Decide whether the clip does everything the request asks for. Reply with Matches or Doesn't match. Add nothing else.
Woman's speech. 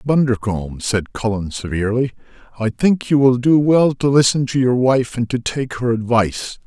Doesn't match